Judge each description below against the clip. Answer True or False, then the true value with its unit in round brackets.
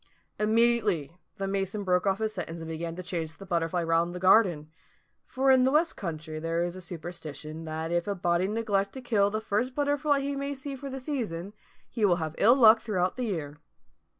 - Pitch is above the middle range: True (195 Hz)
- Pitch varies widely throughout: True (5.7 semitones)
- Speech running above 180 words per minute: True (205 wpm)